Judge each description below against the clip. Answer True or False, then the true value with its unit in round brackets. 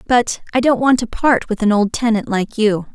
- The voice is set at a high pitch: True (225 Hz)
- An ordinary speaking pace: False (245 wpm)